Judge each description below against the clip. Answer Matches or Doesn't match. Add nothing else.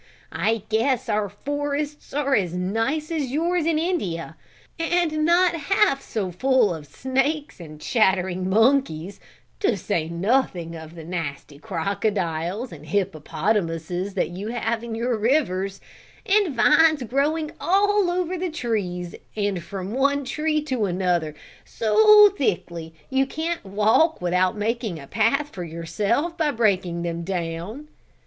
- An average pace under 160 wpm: Matches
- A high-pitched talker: Matches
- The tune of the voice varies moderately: Doesn't match